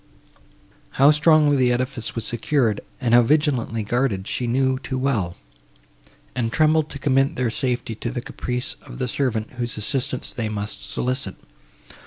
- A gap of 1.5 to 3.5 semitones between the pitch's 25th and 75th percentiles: Yes, average, 2.9 semitones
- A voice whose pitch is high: No, low, 125 Hz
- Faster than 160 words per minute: No, average, 155 wpm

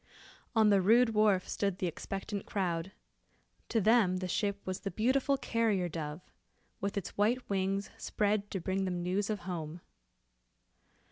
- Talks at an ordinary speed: Yes, average, 150 wpm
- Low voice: No, high, 195 Hz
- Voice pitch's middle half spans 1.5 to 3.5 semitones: Yes, average, 2.7 semitones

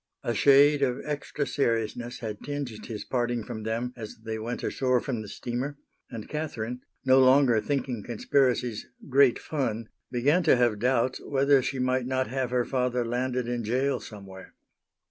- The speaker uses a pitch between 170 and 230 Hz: No, low, 125 Hz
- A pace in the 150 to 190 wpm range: Yes, average, 165 wpm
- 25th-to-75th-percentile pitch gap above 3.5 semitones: No, narrow, 2.5 semitones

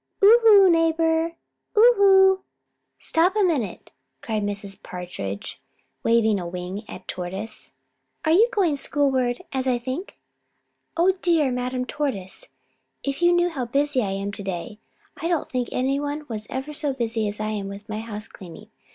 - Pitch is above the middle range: Yes, very high, 255 Hz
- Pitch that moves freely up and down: Yes, wide, 7.8 semitones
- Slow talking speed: No, average, 160 wpm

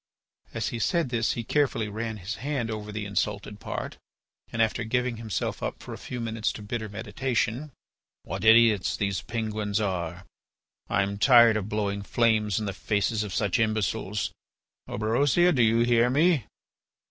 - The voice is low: Yes, low, 110 Hz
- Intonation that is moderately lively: No, narrow, 2.2 semitones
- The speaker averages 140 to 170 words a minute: Yes, average, 165 wpm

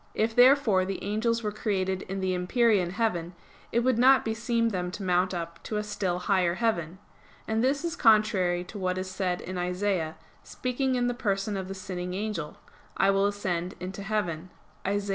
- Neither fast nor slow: Yes, average, 185 wpm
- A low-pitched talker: No, high, 195 Hz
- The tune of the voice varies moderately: Yes, average, 3.5 semitones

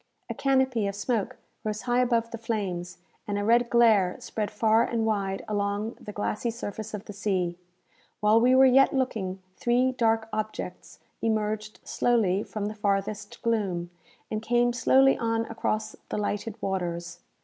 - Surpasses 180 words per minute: No, average, 160 wpm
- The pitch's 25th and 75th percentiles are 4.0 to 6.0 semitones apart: No, narrow, 2.6 semitones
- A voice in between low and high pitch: No, high, 215 Hz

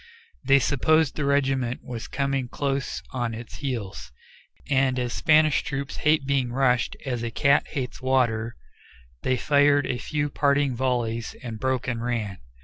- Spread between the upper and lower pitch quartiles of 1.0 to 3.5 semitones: Yes, narrow, 2.6 semitones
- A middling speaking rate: Yes, average, 150 wpm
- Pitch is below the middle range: Yes, low, 130 Hz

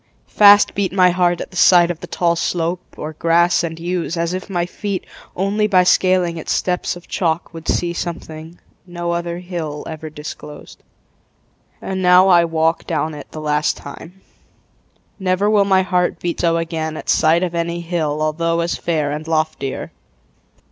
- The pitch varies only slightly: Yes, narrow, 2.1 semitones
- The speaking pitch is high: No, medium, 170 Hz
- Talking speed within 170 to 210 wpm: Yes, average, 175 wpm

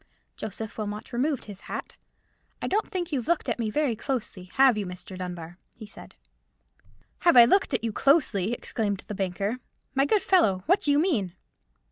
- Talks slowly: No, average, 180 wpm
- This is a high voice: Yes, high, 230 Hz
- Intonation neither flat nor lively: No, wide, 6.2 semitones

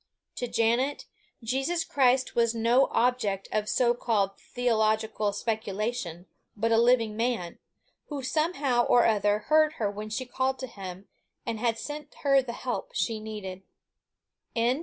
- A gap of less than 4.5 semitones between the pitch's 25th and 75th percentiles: Yes, average, 3.4 semitones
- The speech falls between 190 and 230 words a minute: No, average, 140 wpm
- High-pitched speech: Yes, high, 230 Hz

